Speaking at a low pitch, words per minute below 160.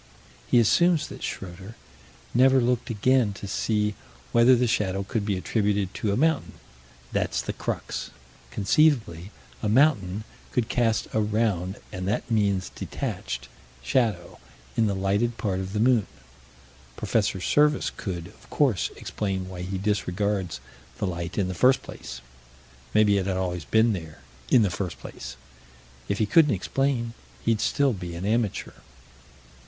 Yes: low, 105 Hz; average, 150 wpm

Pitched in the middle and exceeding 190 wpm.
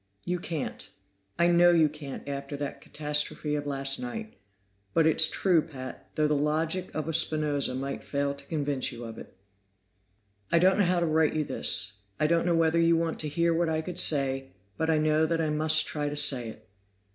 Yes: medium, 155 Hz; fast, 205 wpm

